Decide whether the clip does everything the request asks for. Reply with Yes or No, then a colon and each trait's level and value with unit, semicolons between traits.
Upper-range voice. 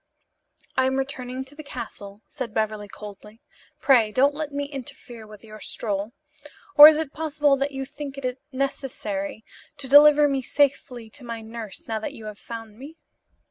Yes: very high, 260 Hz